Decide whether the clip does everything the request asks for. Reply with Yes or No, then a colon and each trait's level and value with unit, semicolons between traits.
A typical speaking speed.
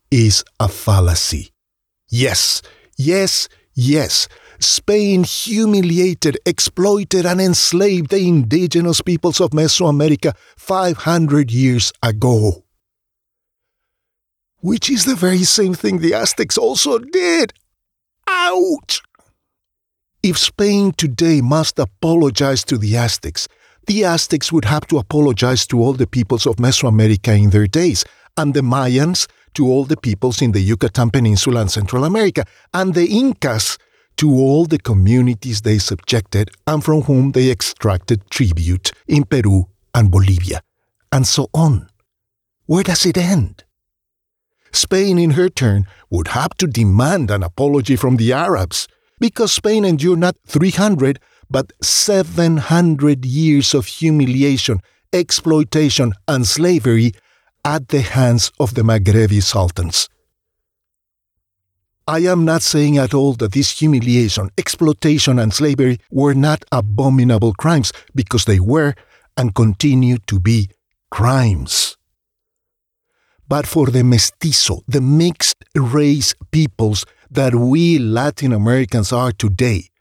No: slow, 125 wpm